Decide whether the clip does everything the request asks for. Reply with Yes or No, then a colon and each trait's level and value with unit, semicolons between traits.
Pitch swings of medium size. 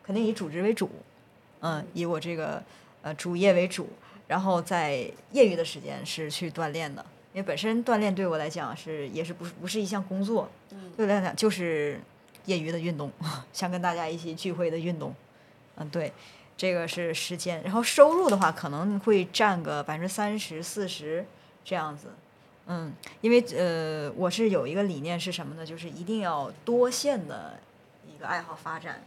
Yes: average, 3.7 semitones